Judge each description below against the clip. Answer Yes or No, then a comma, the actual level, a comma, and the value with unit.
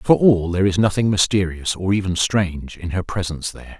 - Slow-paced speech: No, fast, 205 wpm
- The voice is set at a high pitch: No, very low, 95 Hz